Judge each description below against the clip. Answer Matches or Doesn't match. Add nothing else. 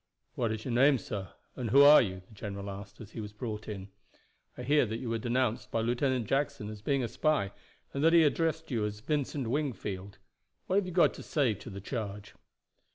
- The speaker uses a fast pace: Matches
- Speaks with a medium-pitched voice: Doesn't match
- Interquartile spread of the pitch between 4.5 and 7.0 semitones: Matches